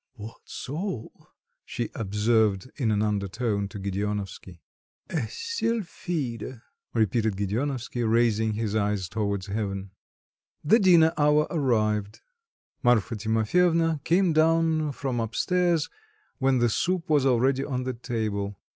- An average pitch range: No, wide, 6.3 semitones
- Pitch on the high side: No, low, 120 Hz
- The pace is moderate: No, slow, 120 wpm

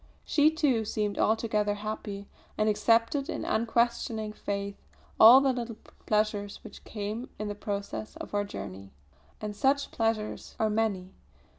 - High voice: Yes, high, 215 Hz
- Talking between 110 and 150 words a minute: Yes, average, 140 wpm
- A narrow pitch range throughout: Yes, narrow, 2.0 semitones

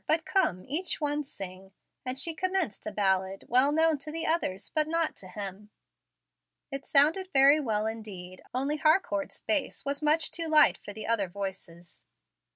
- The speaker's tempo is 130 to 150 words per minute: No, average, 165 wpm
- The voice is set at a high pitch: Yes, very high, 275 Hz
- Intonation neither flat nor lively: No, wide, 7.8 semitones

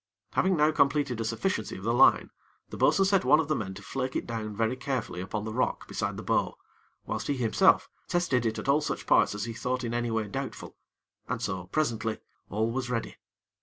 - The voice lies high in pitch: No, low, 120 Hz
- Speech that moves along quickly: Yes, fast, 215 wpm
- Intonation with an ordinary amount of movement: Yes, average, 4.2 semitones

